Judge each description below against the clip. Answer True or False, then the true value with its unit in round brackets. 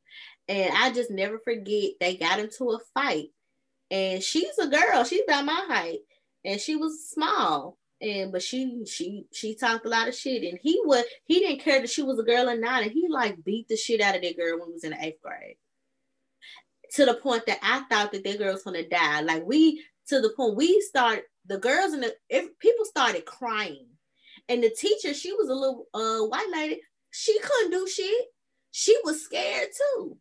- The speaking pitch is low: False (250 Hz)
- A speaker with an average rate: False (215 wpm)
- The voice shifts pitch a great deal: True (7.8 semitones)